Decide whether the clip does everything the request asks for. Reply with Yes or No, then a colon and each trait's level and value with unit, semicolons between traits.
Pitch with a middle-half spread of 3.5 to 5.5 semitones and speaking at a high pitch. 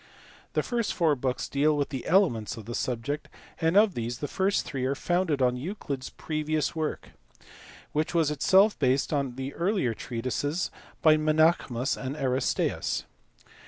No: average, 4.2 semitones; medium, 145 Hz